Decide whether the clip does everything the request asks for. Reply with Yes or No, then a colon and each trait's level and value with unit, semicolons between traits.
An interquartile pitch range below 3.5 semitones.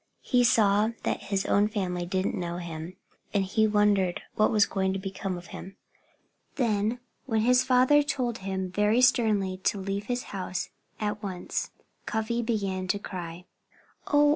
Yes: average, 3.0 semitones